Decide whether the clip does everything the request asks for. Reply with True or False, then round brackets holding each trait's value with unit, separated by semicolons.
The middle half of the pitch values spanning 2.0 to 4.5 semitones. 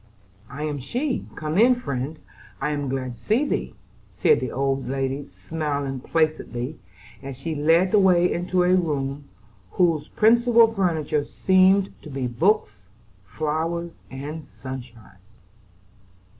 False (5.2 semitones)